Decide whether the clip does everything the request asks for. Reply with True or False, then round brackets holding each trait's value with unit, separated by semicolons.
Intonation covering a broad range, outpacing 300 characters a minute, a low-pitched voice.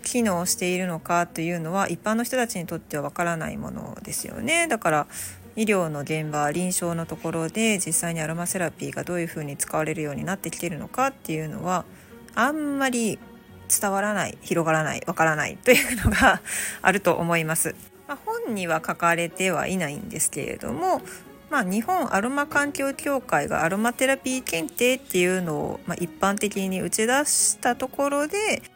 False (6.3 semitones; 380 characters per minute; 185 Hz)